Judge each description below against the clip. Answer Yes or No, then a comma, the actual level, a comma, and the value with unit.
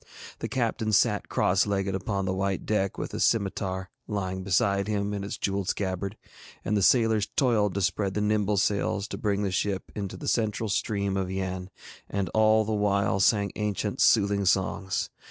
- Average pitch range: No, narrow, 1.6 semitones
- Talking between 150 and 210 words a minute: Yes, average, 180 wpm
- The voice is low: Yes, low, 100 Hz